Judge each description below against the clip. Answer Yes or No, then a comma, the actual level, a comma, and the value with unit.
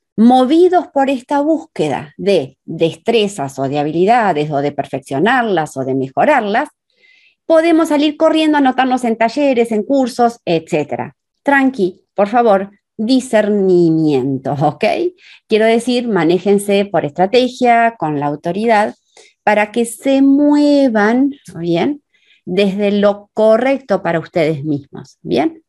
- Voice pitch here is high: Yes, high, 215 Hz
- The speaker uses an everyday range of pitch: No, wide, 8.4 semitones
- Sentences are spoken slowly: Yes, slow, 115 wpm